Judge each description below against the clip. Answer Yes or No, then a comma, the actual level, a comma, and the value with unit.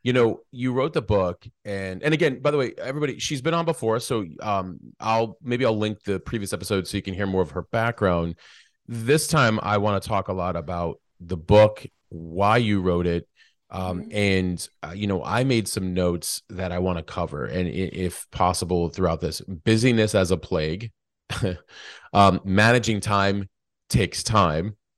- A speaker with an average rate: Yes, average, 185 wpm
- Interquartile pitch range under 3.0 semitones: No, average, 3.9 semitones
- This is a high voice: No, low, 100 Hz